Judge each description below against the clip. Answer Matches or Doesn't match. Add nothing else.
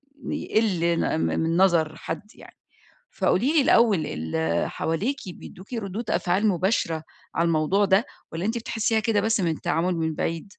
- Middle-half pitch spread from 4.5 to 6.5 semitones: Matches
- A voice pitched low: Doesn't match